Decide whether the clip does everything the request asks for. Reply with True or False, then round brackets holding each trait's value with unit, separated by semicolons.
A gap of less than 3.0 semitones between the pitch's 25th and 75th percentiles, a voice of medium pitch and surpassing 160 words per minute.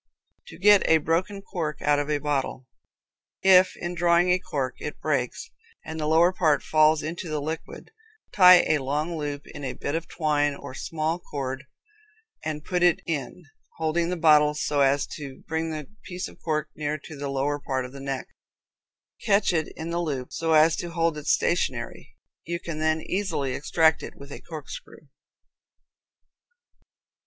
True (2.6 semitones; 155 Hz; 175 wpm)